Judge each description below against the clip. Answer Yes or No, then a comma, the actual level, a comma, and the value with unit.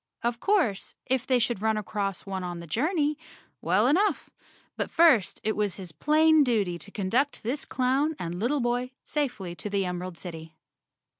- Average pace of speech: Yes, average, 170 wpm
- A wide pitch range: Yes, wide, 6.8 semitones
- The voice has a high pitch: Yes, high, 220 Hz